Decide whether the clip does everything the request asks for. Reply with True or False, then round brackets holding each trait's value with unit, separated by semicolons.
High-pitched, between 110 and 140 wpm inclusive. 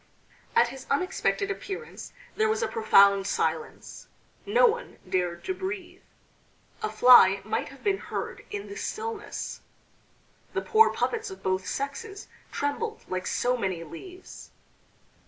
True (365 Hz; 135 wpm)